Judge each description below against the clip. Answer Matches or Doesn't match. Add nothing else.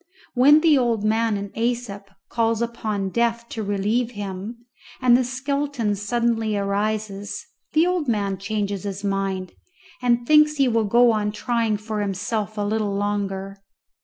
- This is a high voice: Matches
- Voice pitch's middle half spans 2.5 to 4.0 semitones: Matches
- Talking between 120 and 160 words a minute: Matches